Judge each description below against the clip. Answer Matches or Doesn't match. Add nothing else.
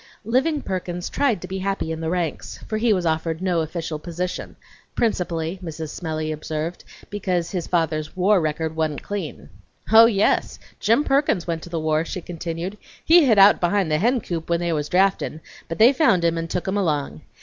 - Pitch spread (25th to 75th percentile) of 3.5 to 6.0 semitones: Matches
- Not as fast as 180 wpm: Doesn't match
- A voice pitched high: Doesn't match